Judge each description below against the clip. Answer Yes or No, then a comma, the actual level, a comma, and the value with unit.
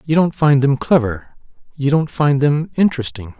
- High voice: No, medium, 140 Hz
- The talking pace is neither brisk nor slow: Yes, average, 175 wpm